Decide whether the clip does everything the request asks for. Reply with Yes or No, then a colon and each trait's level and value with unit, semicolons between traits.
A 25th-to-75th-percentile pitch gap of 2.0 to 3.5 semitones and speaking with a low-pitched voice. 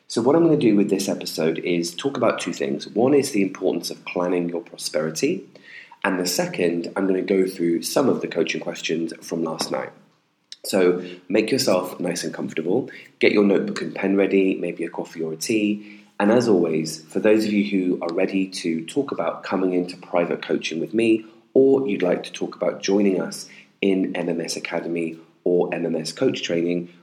Yes: average, 2.8 semitones; very low, 90 Hz